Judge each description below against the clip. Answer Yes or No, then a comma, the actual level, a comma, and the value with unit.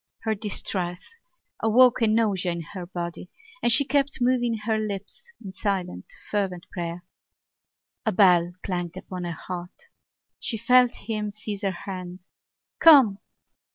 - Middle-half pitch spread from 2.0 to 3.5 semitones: No, average, 4.1 semitones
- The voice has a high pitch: Yes, high, 200 Hz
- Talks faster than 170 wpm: No, slow, 135 wpm